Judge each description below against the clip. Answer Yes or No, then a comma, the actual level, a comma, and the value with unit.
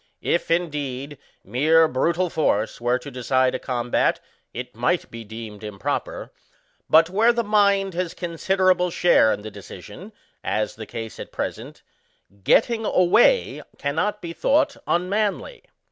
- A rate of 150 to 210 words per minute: No, average, 140 wpm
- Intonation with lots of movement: Yes, wide, 7.3 semitones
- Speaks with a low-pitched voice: No, medium, 160 Hz